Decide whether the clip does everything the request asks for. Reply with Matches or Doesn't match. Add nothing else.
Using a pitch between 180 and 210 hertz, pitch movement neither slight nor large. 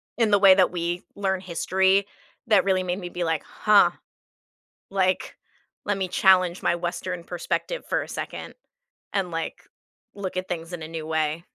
Doesn't match